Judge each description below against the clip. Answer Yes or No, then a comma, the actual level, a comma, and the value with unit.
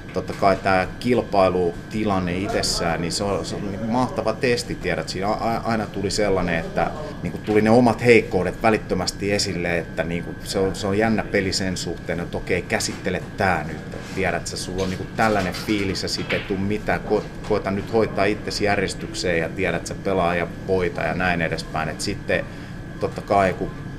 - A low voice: Yes, low, 100 Hz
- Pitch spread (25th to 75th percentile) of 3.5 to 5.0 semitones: No, average, 2.7 semitones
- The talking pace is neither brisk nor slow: No, fast, 190 wpm